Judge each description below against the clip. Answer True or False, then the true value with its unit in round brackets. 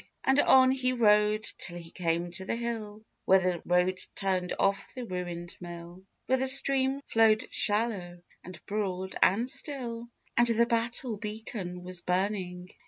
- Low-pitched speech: False (205 Hz)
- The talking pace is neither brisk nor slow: True (160 wpm)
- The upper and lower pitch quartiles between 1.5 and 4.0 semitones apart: False (4.6 semitones)